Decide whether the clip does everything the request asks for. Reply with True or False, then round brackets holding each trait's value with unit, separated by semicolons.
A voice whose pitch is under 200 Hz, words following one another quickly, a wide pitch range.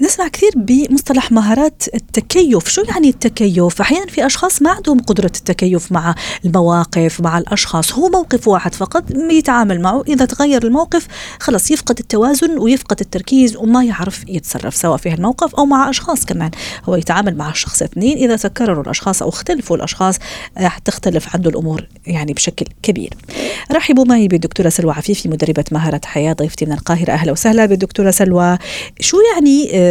False (205 Hz; 155 wpm; 8.0 semitones)